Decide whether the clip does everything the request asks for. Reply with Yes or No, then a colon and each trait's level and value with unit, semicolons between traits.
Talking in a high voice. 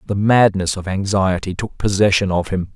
No: very low, 95 Hz